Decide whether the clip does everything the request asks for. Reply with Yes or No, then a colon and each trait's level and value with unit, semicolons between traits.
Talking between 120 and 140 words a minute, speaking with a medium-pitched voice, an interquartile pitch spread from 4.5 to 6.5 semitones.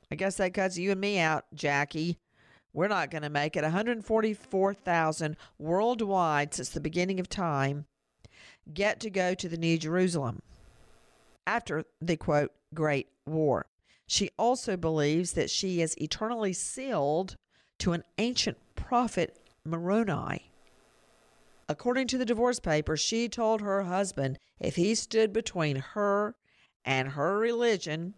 Yes: slow, 135 wpm; medium, 180 Hz; average, 5.1 semitones